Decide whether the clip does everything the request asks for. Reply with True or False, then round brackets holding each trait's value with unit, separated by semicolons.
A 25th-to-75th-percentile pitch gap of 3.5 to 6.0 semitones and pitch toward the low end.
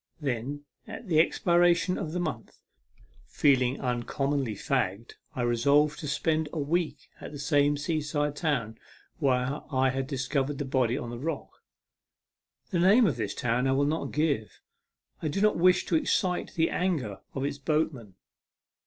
False (3.8 semitones; 145 Hz)